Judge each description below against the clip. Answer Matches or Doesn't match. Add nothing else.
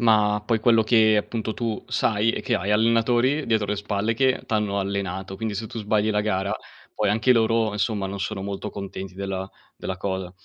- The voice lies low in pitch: Matches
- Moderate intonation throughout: Doesn't match